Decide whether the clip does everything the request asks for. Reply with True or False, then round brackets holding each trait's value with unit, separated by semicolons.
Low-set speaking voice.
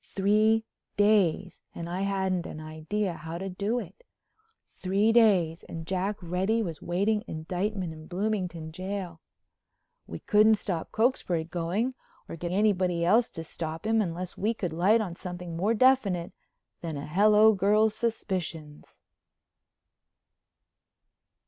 False (190 Hz)